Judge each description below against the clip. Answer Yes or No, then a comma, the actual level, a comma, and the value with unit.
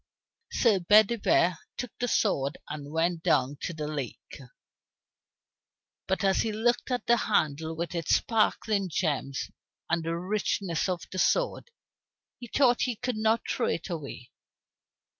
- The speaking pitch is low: No, medium, 185 Hz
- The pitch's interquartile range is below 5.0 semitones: No, wide, 5.5 semitones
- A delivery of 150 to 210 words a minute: No, average, 140 wpm